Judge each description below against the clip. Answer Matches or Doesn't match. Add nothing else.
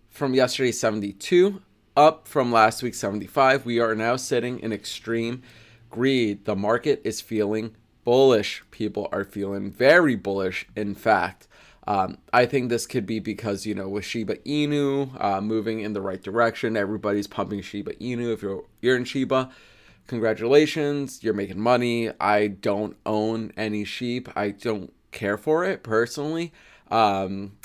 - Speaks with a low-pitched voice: Matches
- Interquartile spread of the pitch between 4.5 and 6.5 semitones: Doesn't match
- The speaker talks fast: Doesn't match